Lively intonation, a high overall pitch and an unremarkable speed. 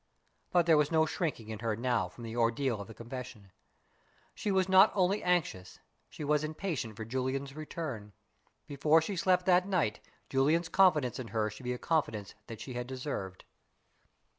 No: wide, 6.4 semitones; low, 135 Hz; average, 175 wpm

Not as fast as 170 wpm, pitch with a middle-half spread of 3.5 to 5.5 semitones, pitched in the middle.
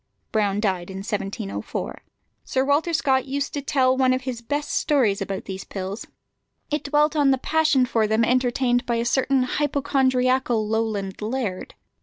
No: average, 160 wpm; average, 4.2 semitones; very high, 255 Hz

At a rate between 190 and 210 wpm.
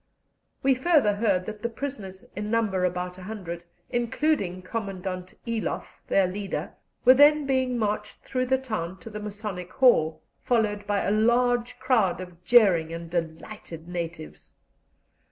No: average, 145 wpm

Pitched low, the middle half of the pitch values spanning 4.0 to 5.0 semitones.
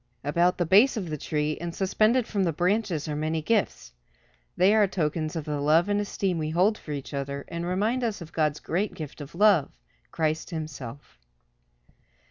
No: medium, 170 Hz; average, 4.7 semitones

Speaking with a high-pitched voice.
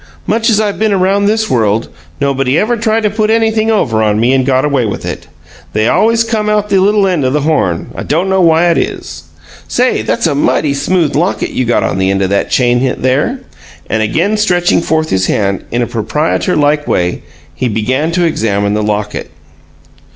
No: medium, 150 Hz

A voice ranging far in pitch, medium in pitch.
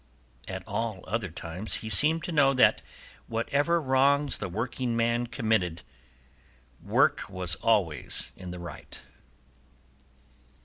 No: wide, 6.4 semitones; low, 115 Hz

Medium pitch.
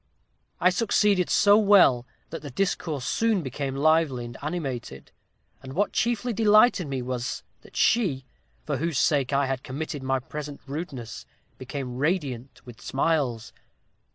Yes: medium, 145 Hz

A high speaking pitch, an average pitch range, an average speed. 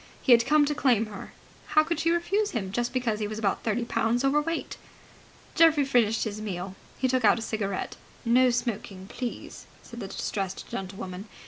Yes: high, 235 Hz; average, 4.8 semitones; average, 185 wpm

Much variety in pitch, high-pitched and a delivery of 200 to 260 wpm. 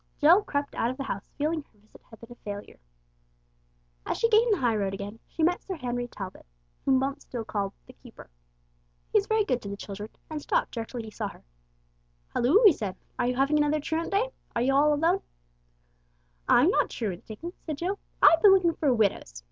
Yes: wide, 7.3 semitones; very high, 270 Hz; fast, 205 wpm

